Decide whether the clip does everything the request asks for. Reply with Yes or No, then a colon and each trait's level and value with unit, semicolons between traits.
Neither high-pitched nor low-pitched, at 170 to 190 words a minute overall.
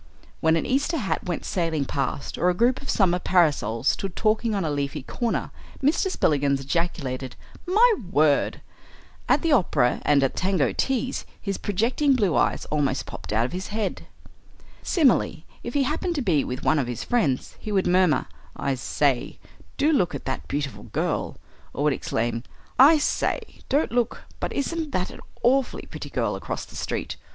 Yes: medium, 180 Hz; average, 175 wpm